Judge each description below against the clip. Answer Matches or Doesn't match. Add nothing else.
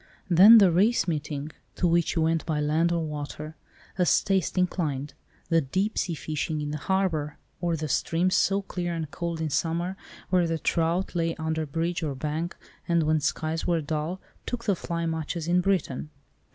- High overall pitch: Doesn't match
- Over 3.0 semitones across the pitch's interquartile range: Doesn't match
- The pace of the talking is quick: Doesn't match